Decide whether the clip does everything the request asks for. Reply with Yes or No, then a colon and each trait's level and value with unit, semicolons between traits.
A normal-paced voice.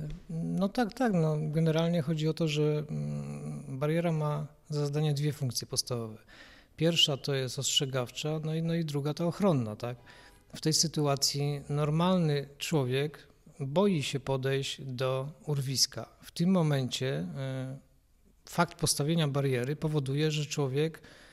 Yes: average, 130 wpm